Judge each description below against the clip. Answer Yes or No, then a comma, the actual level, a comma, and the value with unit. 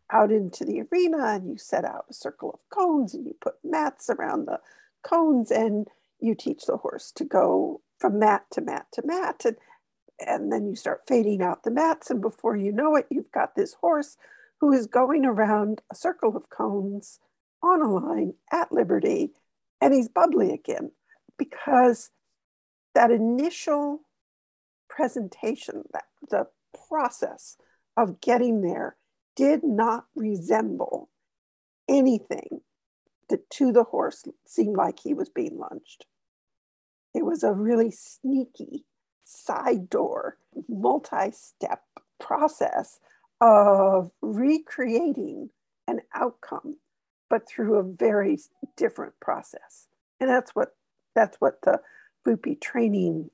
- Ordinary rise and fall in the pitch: No, wide, 6.6 semitones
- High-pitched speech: Yes, very high, 275 Hz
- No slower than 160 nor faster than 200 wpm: No, slow, 135 wpm